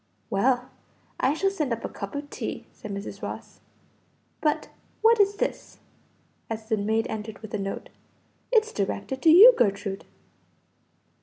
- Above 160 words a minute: No, average, 150 wpm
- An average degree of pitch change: No, wide, 7.6 semitones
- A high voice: Yes, high, 230 Hz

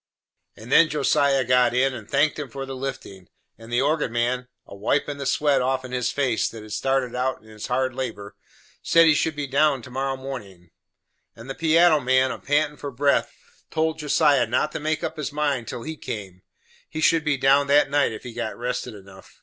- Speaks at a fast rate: Yes, fast, 210 wpm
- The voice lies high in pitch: No, low, 135 Hz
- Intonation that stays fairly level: No, average, 3.4 semitones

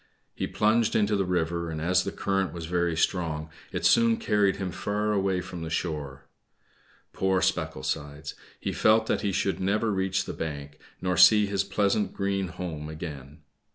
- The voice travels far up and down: No, average, 3.7 semitones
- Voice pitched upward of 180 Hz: No, very low, 90 Hz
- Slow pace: No, average, 170 wpm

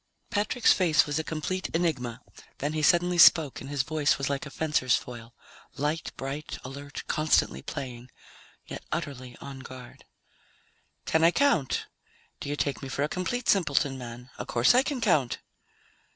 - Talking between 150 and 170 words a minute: Yes, average, 165 wpm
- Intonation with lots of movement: No, average, 3.9 semitones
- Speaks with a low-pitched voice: No, medium, 145 Hz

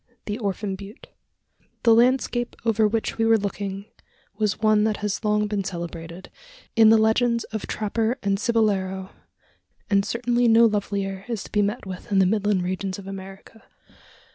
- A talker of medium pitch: No, high, 210 Hz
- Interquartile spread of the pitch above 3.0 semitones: No, narrow, 2.4 semitones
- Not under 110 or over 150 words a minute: No, average, 165 wpm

